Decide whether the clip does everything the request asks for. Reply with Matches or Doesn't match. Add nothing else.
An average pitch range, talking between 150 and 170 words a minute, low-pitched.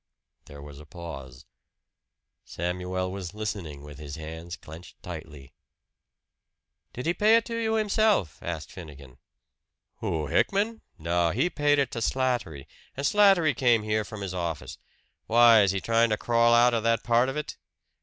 Doesn't match